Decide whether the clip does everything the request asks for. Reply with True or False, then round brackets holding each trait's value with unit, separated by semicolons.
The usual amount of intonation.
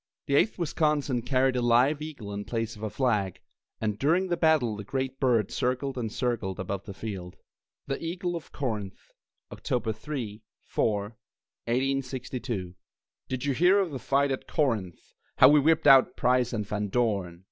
True (4.8 semitones)